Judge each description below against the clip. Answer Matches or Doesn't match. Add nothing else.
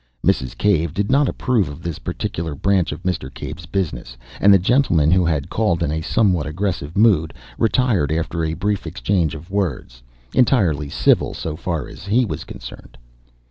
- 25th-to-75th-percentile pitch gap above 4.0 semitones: Matches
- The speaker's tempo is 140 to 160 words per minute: Doesn't match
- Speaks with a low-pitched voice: Matches